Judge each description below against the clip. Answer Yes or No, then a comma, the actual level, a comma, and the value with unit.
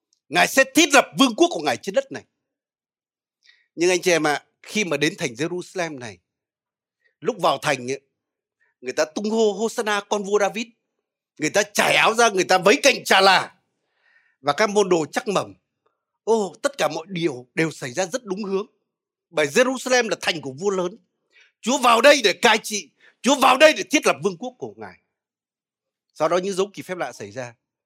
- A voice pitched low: No, high, 205 Hz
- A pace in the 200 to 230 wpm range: Yes, average, 205 wpm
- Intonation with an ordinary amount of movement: No, wide, 6.9 semitones